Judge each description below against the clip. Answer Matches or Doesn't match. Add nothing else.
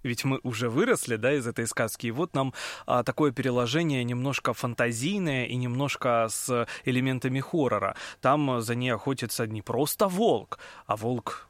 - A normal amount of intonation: Doesn't match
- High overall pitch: Doesn't match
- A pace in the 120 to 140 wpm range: Doesn't match